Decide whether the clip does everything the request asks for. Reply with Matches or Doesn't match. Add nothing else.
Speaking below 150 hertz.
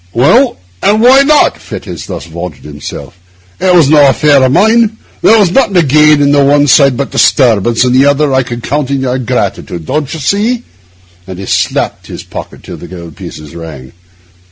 Matches